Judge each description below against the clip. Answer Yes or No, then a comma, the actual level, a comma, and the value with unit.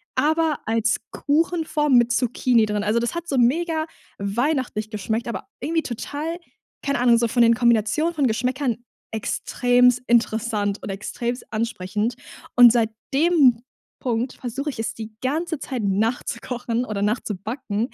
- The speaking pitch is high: Yes, high, 240 Hz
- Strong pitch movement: No, average, 4.0 semitones